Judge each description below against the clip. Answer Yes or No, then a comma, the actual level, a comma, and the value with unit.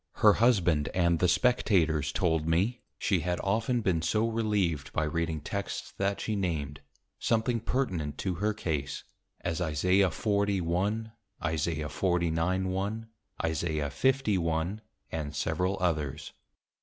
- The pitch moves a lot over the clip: No, average, 4.5 semitones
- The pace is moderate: No, slow, 120 wpm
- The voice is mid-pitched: No, very low, 90 Hz